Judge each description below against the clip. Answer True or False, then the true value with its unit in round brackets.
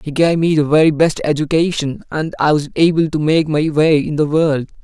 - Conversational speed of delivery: False (225 wpm)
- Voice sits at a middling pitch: True (155 Hz)